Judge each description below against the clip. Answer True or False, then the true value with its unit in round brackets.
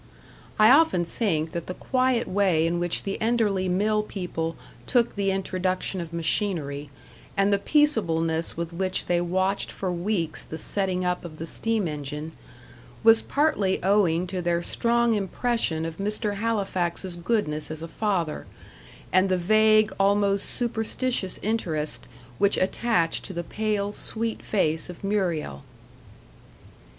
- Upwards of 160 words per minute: False (140 wpm)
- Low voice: False (190 Hz)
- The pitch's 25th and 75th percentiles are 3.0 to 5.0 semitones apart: True (4.1 semitones)